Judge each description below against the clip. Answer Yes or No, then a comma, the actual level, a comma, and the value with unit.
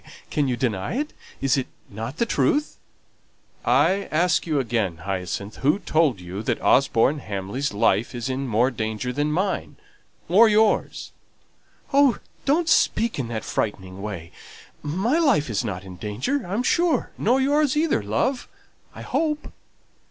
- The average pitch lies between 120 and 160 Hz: Yes, low, 135 Hz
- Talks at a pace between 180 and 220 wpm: No, average, 150 wpm